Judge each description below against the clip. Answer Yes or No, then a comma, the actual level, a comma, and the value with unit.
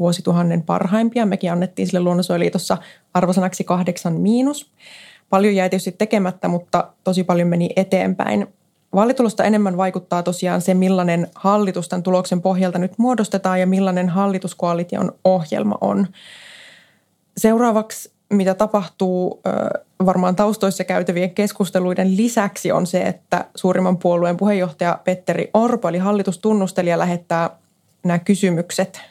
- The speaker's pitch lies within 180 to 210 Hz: Yes, medium, 185 Hz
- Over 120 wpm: No, average, 115 wpm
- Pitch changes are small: Yes, narrow, 2.0 semitones